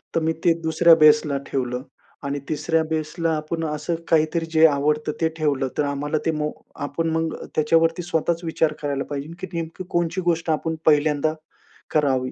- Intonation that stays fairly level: Yes, narrow, 1.8 semitones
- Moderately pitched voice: Yes, medium, 155 Hz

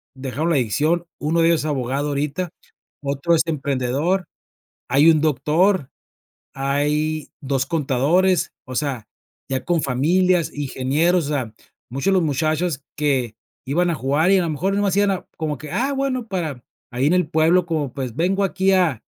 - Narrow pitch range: No, average, 4.3 semitones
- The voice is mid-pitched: Yes, medium, 155 Hz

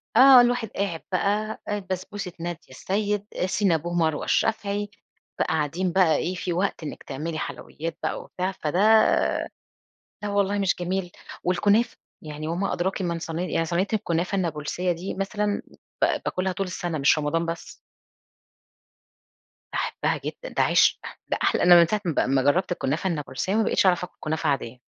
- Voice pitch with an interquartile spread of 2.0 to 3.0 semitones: No, average, 3.4 semitones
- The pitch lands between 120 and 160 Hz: No, medium, 180 Hz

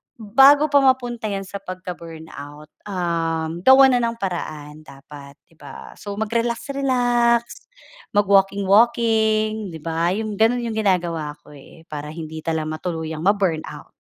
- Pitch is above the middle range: Yes, high, 195 Hz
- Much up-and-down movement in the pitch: Yes, wide, 6.3 semitones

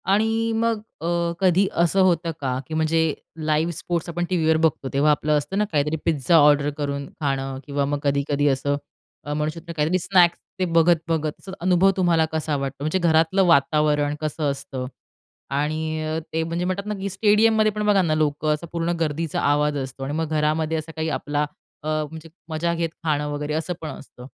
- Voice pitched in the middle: Yes, medium, 155 Hz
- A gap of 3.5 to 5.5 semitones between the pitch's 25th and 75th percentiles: No, average, 2.7 semitones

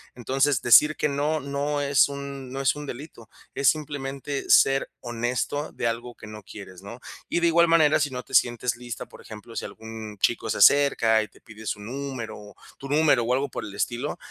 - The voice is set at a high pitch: No, low, 130 Hz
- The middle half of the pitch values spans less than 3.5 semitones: No, average, 3.9 semitones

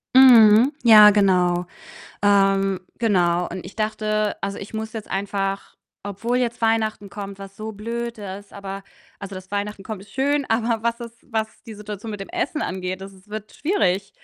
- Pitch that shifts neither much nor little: No, narrow, 2.3 semitones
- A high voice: Yes, high, 210 Hz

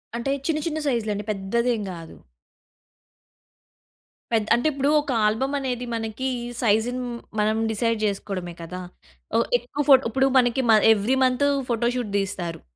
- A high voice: Yes, high, 230 Hz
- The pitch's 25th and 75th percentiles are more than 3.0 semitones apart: Yes, average, 3.6 semitones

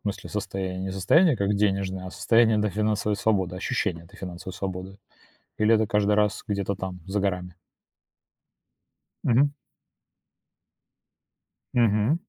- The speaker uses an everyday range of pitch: No, narrow, 2.3 semitones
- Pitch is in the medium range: No, low, 100 Hz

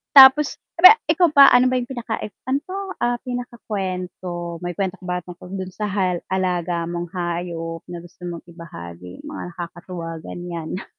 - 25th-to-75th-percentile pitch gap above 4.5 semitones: Yes, average, 5.2 semitones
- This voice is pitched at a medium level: Yes, medium, 180 Hz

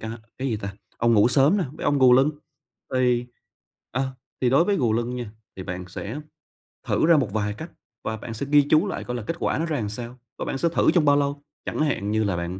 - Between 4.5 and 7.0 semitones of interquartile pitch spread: Yes, average, 5.0 semitones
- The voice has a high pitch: No, low, 125 Hz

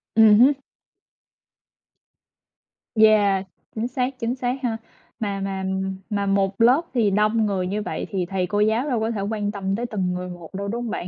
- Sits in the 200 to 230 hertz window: Yes, high, 210 Hz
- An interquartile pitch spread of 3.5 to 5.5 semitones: No, average, 2.8 semitones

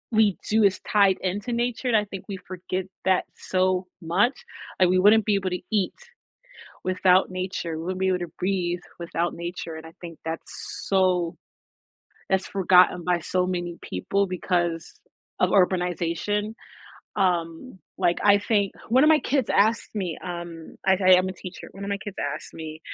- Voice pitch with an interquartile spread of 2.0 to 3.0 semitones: Yes, narrow, 2.5 semitones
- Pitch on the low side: No, medium, 185 Hz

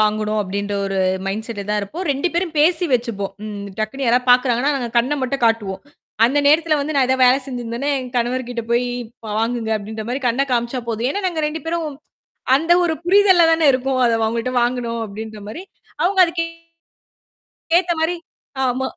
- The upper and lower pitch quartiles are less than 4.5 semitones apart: No, average, 5.3 semitones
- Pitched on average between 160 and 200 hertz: No, very high, 250 Hz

